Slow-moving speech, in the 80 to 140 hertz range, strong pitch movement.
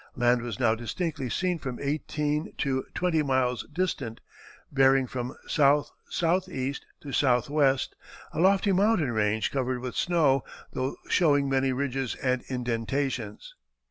No: slow, 125 wpm; low, 135 Hz; average, 3.3 semitones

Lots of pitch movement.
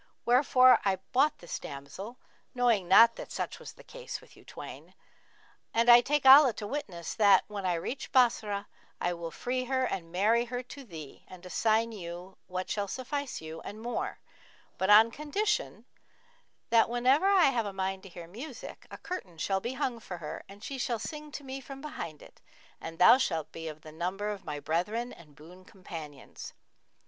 Yes: wide, 6.4 semitones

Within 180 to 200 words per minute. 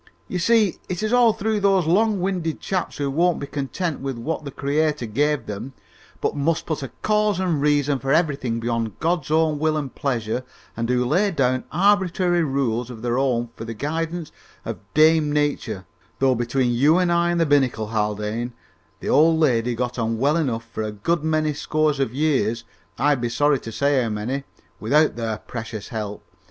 Yes: average, 190 wpm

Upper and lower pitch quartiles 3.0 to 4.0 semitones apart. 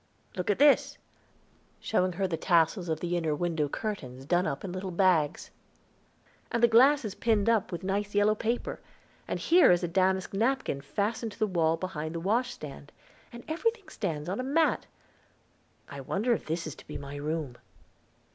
No: wide, 5.5 semitones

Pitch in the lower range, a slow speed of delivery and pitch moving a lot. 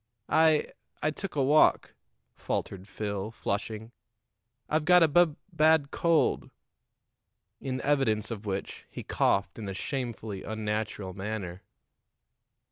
Yes: low, 110 Hz; slow, 120 wpm; wide, 6.8 semitones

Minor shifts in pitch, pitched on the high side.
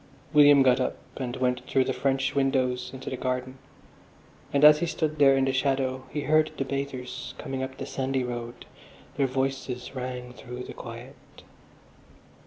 No: narrow, 1.4 semitones; low, 130 Hz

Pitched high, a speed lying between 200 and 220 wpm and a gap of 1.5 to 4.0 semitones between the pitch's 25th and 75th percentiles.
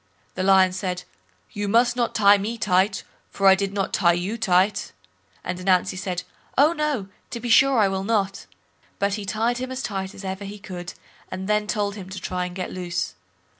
Yes: high, 195 Hz; fast, 205 wpm; narrow, 2.5 semitones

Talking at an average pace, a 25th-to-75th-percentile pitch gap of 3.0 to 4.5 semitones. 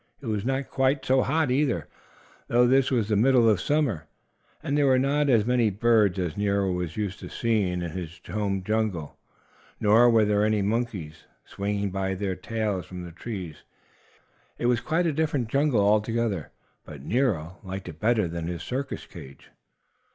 No: average, 175 wpm; average, 5.0 semitones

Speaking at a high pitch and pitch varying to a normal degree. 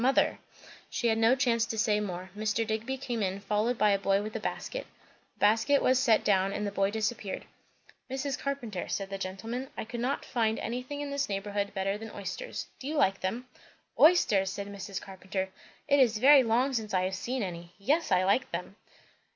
Yes: high, 220 Hz; average, 4.4 semitones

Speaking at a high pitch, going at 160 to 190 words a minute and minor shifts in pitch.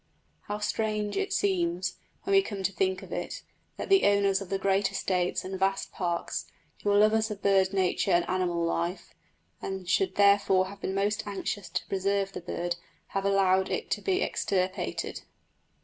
Yes: high, 195 Hz; average, 175 wpm; narrow, 1.6 semitones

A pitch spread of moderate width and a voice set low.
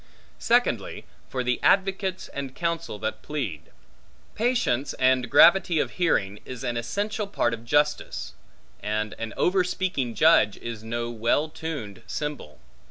No: wide, 6.5 semitones; low, 130 Hz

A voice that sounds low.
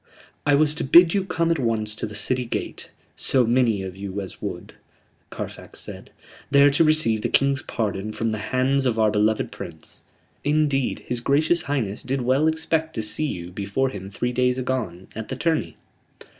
Yes: low, 125 Hz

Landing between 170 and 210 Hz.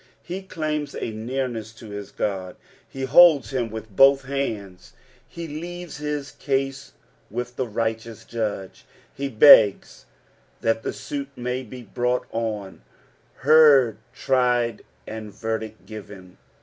No: low, 120 Hz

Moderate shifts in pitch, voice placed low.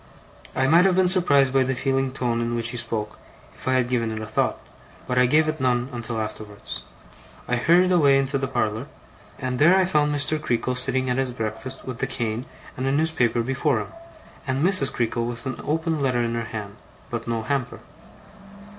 Yes: average, 3.3 semitones; low, 130 Hz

